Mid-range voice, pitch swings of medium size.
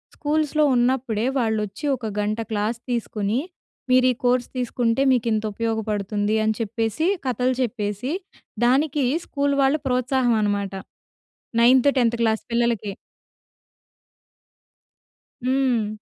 No: high, 235 Hz; average, 3.1 semitones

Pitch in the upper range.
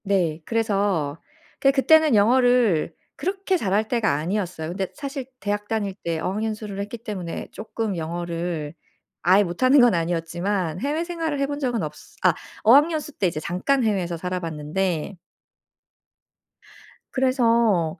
Yes: high, 205 Hz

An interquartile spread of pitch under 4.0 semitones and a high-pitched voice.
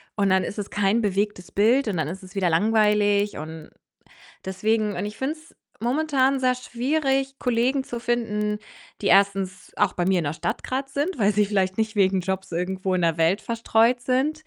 No: average, 4.7 semitones; high, 210 Hz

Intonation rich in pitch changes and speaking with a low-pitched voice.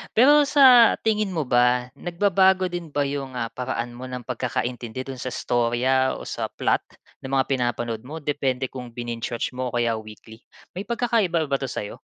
Yes: wide, 6.2 semitones; low, 130 Hz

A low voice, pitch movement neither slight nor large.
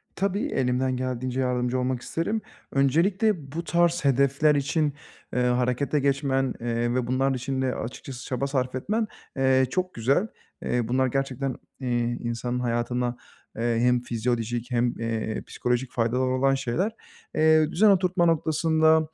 Yes: low, 130 Hz; average, 3.9 semitones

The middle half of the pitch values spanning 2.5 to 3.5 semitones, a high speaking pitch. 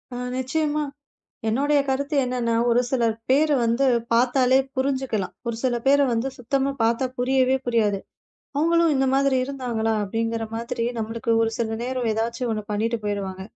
Yes: average, 2.9 semitones; high, 245 Hz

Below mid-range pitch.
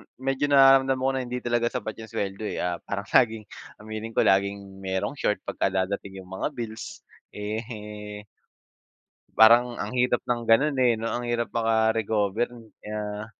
Yes: low, 110 Hz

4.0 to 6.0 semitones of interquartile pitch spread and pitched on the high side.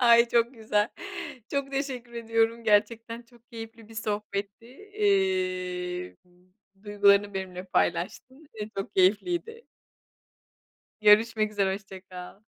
No: average, 3.1 semitones; high, 215 Hz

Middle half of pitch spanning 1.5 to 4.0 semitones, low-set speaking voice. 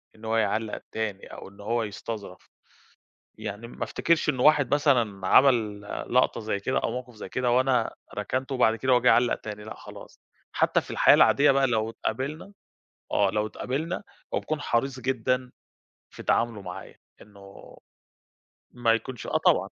Yes: average, 3.5 semitones; low, 120 Hz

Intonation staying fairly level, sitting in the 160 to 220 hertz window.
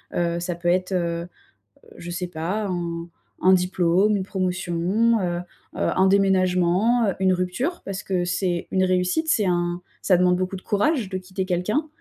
Yes: narrow, 1.9 semitones; medium, 185 Hz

